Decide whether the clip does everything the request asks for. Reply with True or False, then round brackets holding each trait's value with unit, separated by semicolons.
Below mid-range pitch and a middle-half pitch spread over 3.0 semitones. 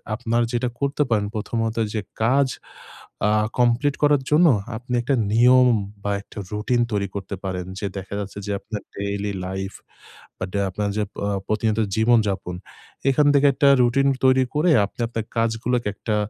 True (115 Hz; 3.7 semitones)